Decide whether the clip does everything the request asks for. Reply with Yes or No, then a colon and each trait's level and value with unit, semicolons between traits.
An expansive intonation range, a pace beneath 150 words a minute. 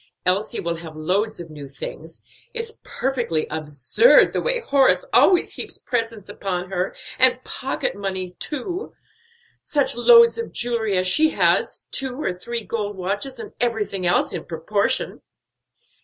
Yes: wide, 6.6 semitones; average, 140 wpm